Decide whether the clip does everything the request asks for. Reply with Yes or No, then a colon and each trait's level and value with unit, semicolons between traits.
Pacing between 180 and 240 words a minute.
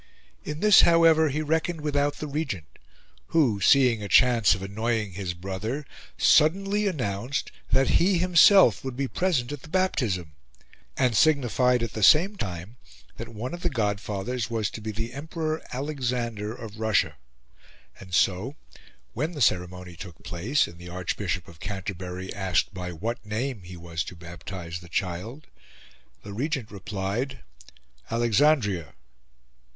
No: average, 145 wpm